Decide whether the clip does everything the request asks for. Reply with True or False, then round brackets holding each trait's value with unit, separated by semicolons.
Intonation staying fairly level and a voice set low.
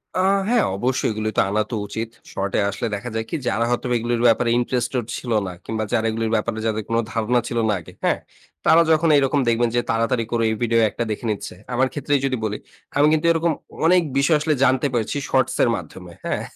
False (3.1 semitones; 120 Hz)